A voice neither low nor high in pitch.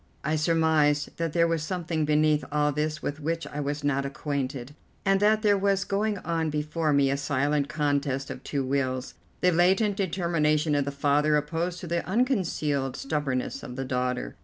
Yes: medium, 150 Hz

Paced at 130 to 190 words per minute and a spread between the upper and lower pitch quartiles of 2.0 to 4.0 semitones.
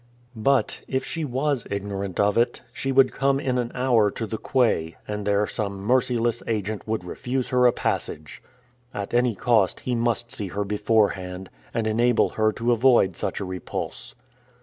Yes: average, 170 wpm; average, 3.5 semitones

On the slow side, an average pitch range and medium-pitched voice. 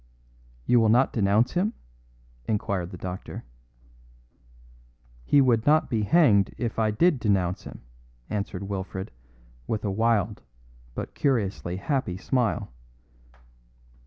No: slow, 115 wpm; average, 4.2 semitones; low, 110 Hz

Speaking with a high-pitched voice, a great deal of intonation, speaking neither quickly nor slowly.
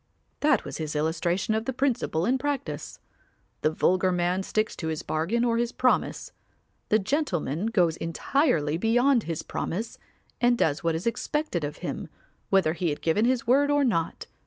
Yes: high, 195 Hz; wide, 7.1 semitones; average, 170 wpm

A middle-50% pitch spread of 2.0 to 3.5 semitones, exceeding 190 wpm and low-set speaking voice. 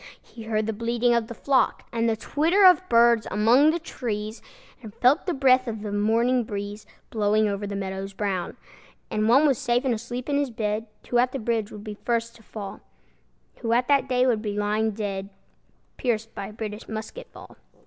No: average, 3.0 semitones; average, 200 wpm; high, 225 Hz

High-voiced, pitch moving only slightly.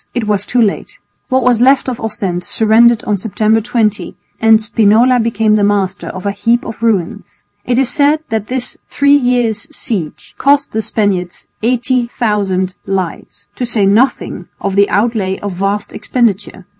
No: high, 220 Hz; average, 3.3 semitones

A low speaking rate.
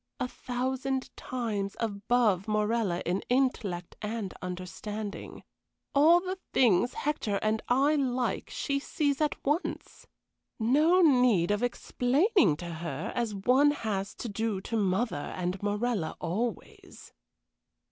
Yes: slow, 115 wpm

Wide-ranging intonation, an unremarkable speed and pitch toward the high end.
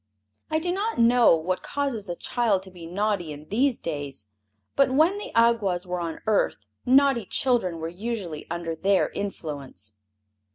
Yes: wide, 6.5 semitones; average, 160 wpm; high, 195 Hz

